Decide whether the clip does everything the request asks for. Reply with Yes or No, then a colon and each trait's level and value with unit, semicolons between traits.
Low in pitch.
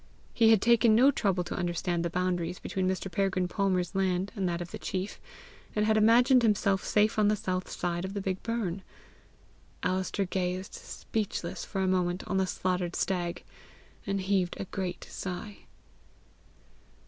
No: high, 190 Hz